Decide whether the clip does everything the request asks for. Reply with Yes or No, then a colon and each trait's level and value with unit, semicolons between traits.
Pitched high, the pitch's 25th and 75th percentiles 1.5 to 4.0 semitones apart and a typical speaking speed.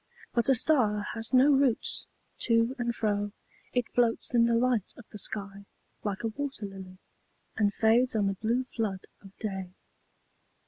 Yes: high, 225 Hz; average, 3.3 semitones; average, 165 wpm